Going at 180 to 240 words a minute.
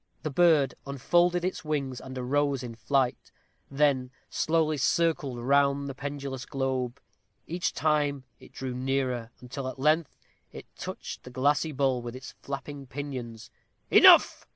No: average, 140 wpm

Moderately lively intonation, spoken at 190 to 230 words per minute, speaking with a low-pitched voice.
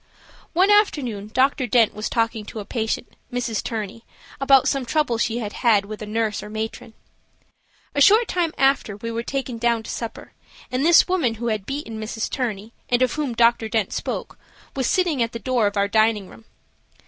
No: average, 3.6 semitones; average, 195 wpm; high, 230 Hz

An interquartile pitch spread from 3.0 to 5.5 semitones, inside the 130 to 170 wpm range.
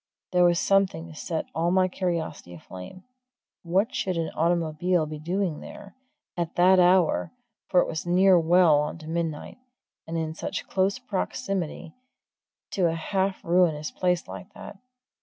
No: narrow, 2.6 semitones; average, 160 wpm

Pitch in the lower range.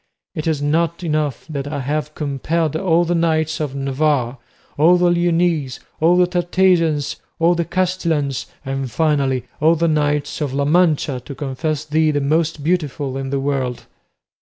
No: medium, 155 Hz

